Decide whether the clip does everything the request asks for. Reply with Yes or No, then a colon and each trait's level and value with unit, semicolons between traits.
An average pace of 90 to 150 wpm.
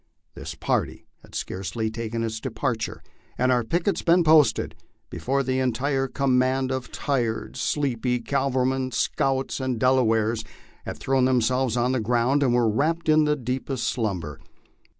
Yes: average, 145 wpm